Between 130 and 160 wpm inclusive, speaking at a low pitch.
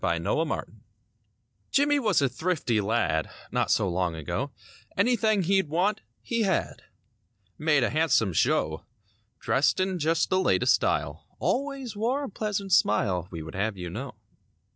No: average, 150 wpm; medium, 165 Hz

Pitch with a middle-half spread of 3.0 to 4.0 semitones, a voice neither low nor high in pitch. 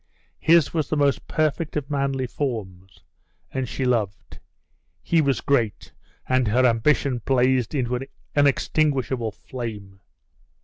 No: average, 3.6 semitones; low, 130 Hz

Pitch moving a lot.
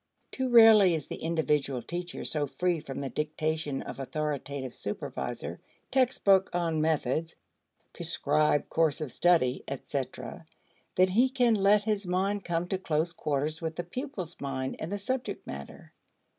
No: average, 4.8 semitones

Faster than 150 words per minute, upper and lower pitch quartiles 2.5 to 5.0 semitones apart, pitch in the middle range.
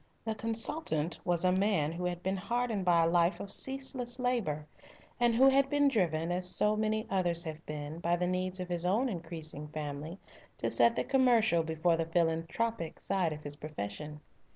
No: average, 185 wpm; wide, 5.4 semitones; medium, 180 Hz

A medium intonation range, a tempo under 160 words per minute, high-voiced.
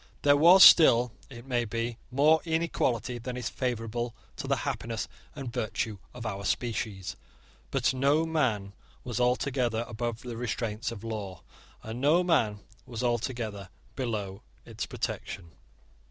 No: average, 3.0 semitones; average, 140 wpm; low, 120 Hz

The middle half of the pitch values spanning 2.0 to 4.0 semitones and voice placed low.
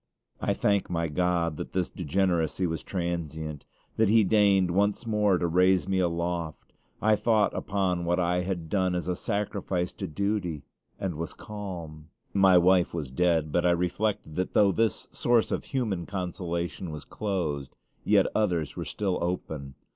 Yes: average, 2.8 semitones; very low, 90 Hz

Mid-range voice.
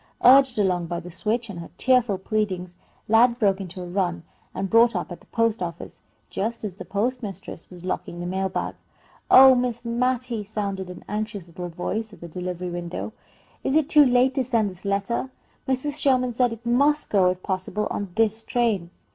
No: high, 210 Hz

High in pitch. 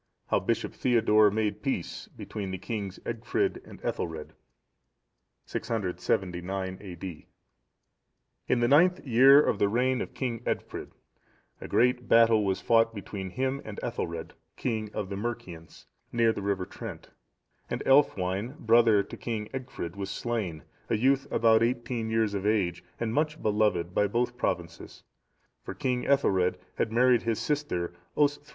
No: low, 110 Hz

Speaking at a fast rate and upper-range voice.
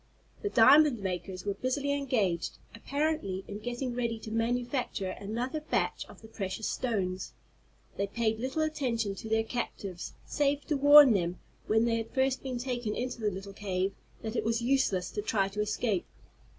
No: average, 170 wpm; high, 225 Hz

